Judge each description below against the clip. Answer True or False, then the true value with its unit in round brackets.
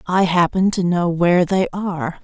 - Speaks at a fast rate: False (190 wpm)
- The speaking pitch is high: False (180 Hz)